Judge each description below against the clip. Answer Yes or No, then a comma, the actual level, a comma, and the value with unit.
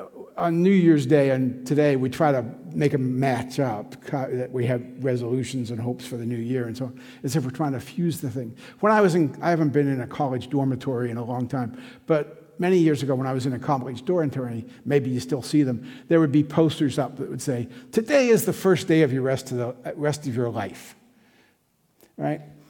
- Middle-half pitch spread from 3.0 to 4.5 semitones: Yes, average, 3.5 semitones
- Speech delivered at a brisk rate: Yes, fast, 235 wpm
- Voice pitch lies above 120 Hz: Yes, low, 135 Hz